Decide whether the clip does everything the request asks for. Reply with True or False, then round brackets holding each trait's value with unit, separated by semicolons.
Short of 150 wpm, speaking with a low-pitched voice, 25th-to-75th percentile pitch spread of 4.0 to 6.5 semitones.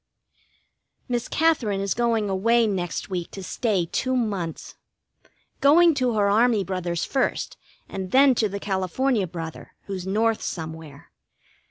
False (135 wpm; 205 Hz; 4.6 semitones)